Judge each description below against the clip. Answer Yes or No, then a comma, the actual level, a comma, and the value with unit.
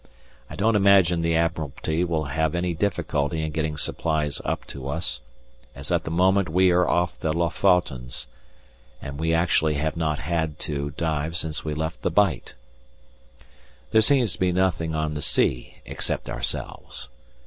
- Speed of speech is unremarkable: Yes, average, 160 wpm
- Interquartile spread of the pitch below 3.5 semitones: Yes, narrow, 2.4 semitones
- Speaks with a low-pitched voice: Yes, very low, 80 Hz